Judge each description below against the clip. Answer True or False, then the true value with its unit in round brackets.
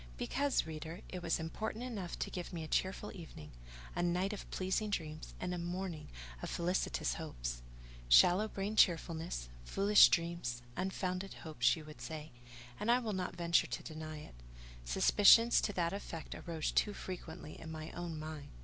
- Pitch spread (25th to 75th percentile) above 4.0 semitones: False (3.5 semitones)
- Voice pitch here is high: False (170 Hz)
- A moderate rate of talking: True (165 wpm)